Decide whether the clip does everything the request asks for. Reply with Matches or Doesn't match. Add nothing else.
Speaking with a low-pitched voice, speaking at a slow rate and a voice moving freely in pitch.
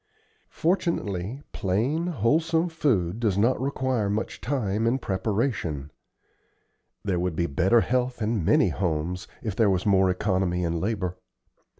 Matches